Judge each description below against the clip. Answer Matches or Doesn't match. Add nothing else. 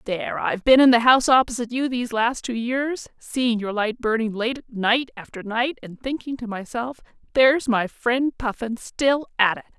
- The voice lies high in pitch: Matches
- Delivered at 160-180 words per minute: Doesn't match